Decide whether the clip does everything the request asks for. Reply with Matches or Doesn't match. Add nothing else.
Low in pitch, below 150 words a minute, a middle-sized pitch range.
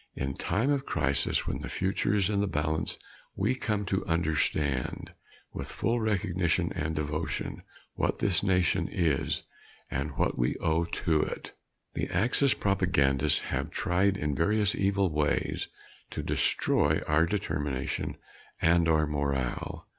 Matches